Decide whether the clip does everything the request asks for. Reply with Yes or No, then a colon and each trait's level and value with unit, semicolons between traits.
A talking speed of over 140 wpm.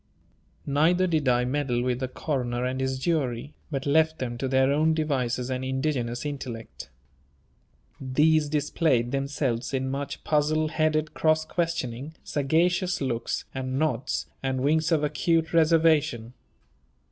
No: slow, 135 wpm